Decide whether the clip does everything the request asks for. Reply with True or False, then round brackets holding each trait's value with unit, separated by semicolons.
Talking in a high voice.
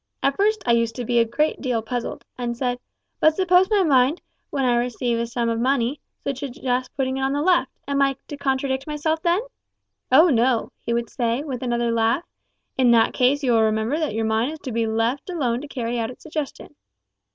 True (255 Hz)